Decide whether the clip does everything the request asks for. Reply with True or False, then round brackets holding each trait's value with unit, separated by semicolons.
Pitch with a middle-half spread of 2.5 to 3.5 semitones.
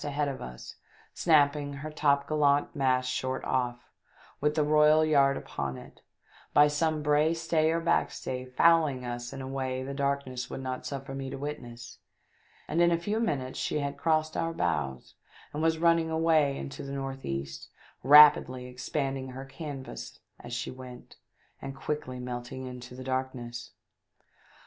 True (2.9 semitones)